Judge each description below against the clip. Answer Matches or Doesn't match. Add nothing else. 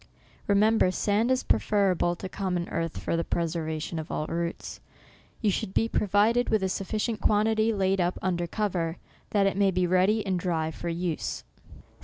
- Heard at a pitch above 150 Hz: Matches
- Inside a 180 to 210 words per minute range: Doesn't match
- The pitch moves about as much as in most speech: Matches